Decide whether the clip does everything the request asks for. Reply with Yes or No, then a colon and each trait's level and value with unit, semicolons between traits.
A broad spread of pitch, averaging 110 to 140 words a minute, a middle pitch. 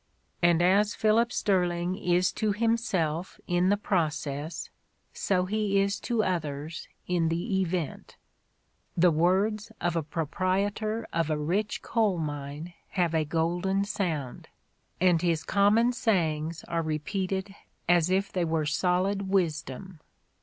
No: average, 3.6 semitones; slow, 135 wpm; medium, 180 Hz